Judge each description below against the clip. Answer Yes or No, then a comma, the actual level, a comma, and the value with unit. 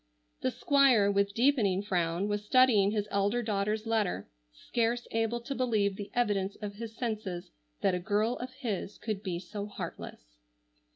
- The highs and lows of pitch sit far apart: No, average, 2.8 semitones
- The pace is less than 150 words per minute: No, average, 160 wpm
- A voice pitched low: No, high, 210 Hz